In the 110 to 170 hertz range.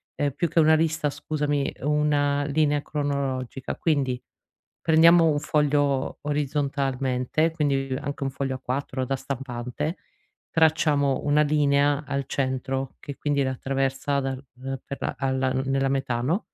Yes: medium, 140 Hz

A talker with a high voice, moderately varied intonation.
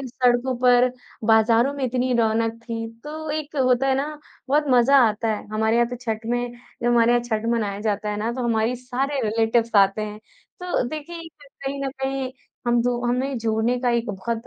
Yes: high, 240 Hz; average, 3.0 semitones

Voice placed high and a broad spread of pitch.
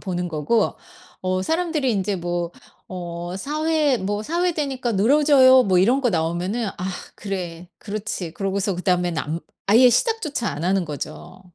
Yes: high, 200 Hz; wide, 6.6 semitones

